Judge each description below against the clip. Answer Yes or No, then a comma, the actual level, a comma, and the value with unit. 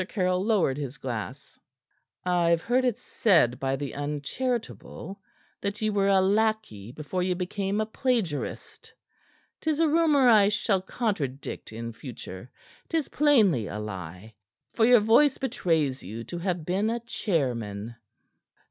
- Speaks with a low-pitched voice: No, medium, 185 Hz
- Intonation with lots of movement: Yes, wide, 8.7 semitones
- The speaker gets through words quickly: No, average, 140 wpm